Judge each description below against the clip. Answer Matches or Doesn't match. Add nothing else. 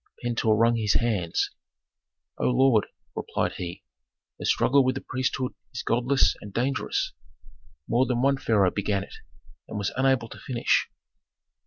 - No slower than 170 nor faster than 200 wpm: Doesn't match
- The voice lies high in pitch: Doesn't match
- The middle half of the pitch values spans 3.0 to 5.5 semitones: Matches